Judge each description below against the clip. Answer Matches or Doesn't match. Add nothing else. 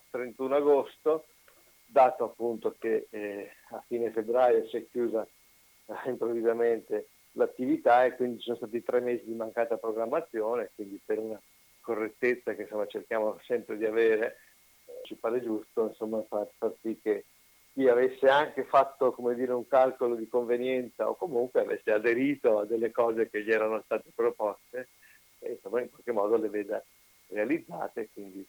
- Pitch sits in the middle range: Doesn't match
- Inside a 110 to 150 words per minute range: Doesn't match